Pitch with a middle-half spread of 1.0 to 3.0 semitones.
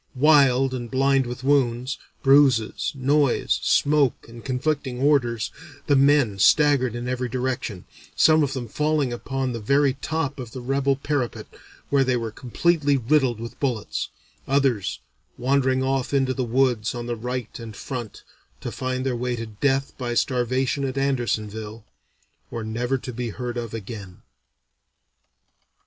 Yes: narrow, 2.5 semitones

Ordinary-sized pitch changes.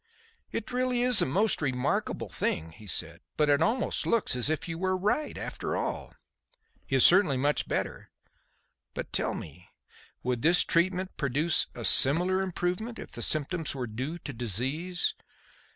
No: wide, 6.2 semitones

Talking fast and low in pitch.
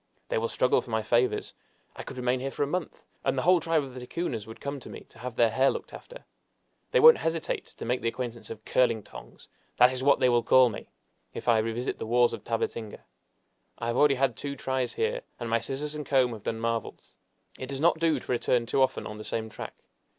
Yes: fast, 240 wpm; low, 125 Hz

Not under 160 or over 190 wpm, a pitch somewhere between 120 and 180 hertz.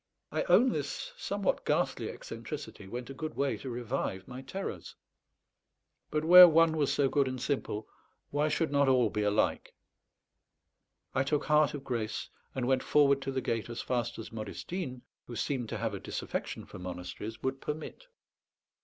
Yes: average, 170 wpm; low, 135 Hz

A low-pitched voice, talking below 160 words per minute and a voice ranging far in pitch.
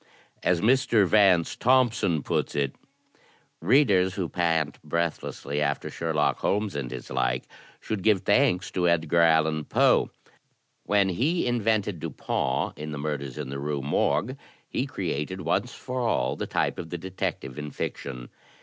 Yes: very low, 85 Hz; average, 150 wpm; wide, 5.7 semitones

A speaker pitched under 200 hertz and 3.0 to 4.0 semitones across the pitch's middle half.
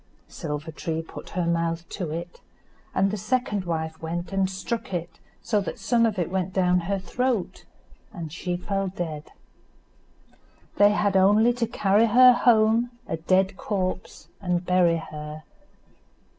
Yes: medium, 185 Hz; average, 3.6 semitones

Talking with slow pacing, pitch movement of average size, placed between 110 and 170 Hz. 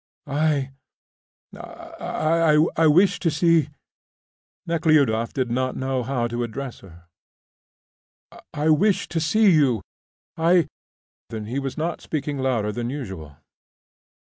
Yes: slow, 120 wpm; average, 4.9 semitones; medium, 140 Hz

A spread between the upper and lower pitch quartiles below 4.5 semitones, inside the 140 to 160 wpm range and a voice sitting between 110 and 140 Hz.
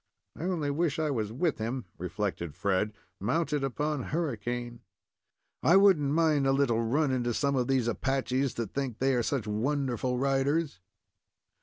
Yes: average, 3.9 semitones; average, 155 wpm; low, 135 Hz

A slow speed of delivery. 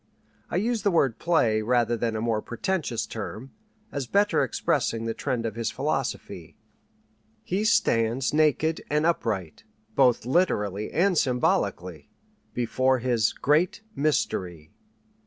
Yes: slow, 125 wpm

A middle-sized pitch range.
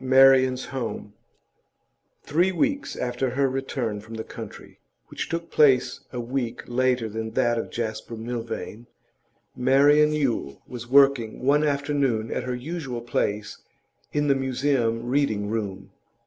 Yes: average, 3.3 semitones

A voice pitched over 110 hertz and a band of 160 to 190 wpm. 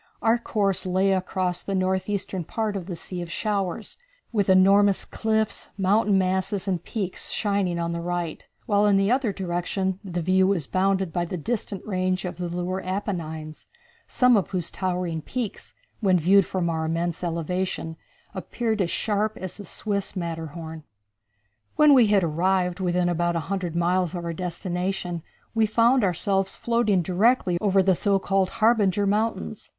Yes: medium, 185 Hz; average, 165 wpm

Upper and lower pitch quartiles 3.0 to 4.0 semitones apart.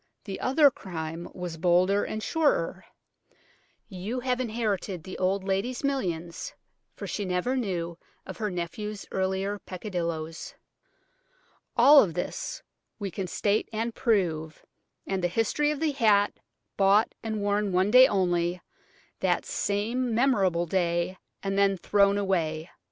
Yes: average, 3.7 semitones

